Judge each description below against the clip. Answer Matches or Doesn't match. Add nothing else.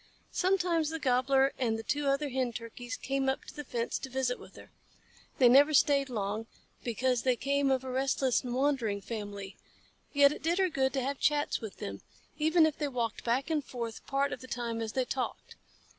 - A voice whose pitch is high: Matches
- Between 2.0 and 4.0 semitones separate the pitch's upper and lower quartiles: Matches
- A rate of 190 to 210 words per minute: Matches